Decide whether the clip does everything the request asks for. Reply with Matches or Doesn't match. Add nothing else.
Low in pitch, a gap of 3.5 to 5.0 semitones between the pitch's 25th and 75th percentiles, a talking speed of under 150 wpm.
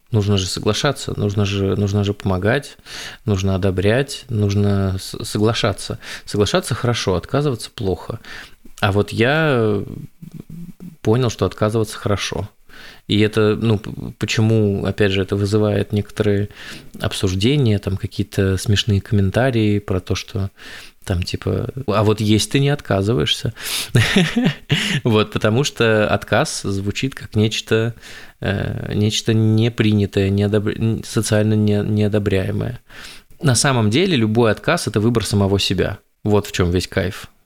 Doesn't match